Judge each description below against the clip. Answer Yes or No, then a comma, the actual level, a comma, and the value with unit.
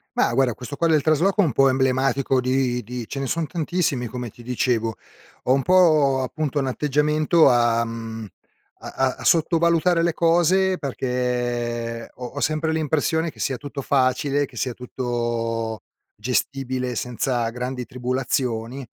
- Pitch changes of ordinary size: Yes, average, 3.8 semitones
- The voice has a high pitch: No, low, 130 Hz